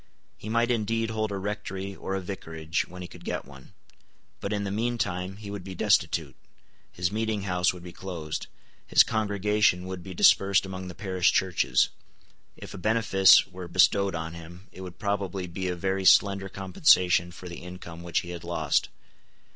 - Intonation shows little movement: Yes, narrow, 2.3 semitones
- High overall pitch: No, very low, 95 Hz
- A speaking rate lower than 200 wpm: Yes, average, 180 wpm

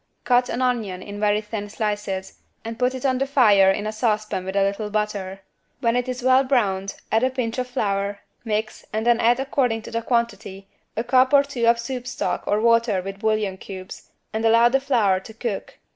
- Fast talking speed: Yes, fast, 210 wpm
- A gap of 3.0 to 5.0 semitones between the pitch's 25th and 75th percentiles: Yes, average, 3.4 semitones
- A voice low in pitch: No, high, 225 Hz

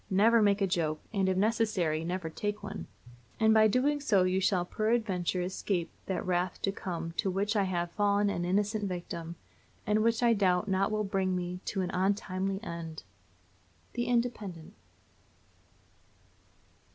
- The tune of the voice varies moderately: Yes, average, 3.0 semitones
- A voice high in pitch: Yes, high, 195 Hz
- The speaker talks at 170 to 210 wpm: No, average, 155 wpm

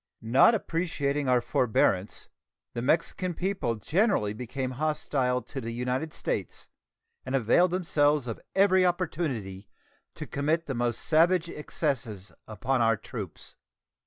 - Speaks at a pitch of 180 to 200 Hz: No, low, 135 Hz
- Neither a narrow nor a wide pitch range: No, wide, 6.0 semitones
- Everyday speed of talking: No, slow, 125 wpm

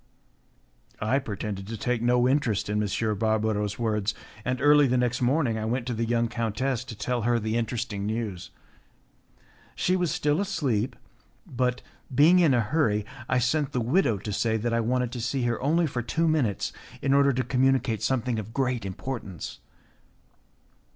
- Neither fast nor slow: Yes, average, 170 wpm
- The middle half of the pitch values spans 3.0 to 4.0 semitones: Yes, average, 3.3 semitones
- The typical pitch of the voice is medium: No, low, 120 Hz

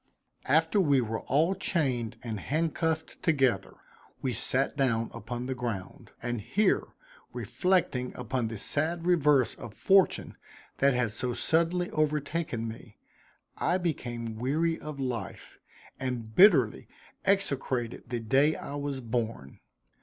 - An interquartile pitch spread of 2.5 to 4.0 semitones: No, average, 5.3 semitones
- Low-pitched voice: Yes, low, 130 Hz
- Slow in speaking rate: Yes, slow, 125 wpm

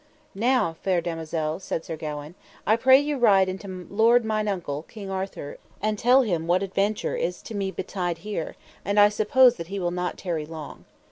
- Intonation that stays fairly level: No, average, 4.2 semitones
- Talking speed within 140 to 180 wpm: No, average, 190 wpm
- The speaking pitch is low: No, high, 190 Hz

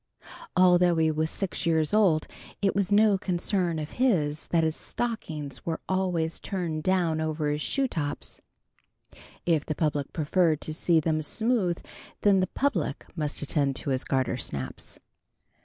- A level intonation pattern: No, average, 3.5 semitones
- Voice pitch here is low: No, medium, 165 Hz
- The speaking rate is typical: Yes, average, 150 wpm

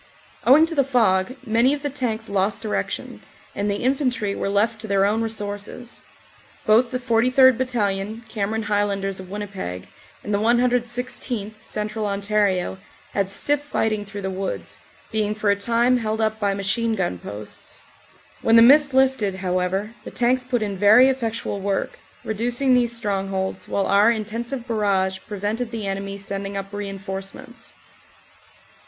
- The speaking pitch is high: Yes, high, 215 Hz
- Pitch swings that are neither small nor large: Yes, average, 3.2 semitones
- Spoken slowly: No, average, 155 wpm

